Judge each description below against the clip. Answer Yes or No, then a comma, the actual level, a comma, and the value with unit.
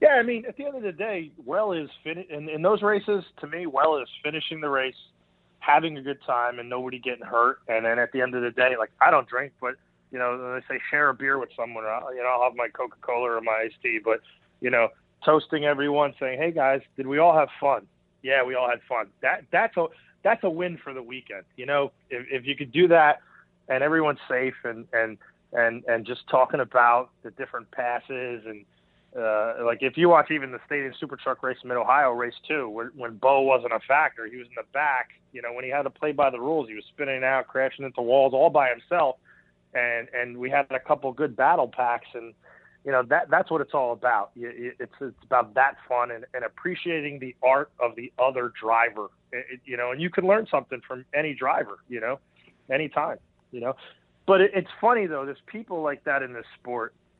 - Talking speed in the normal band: No, fast, 235 wpm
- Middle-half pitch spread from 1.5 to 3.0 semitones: No, average, 3.6 semitones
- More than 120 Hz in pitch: Yes, low, 130 Hz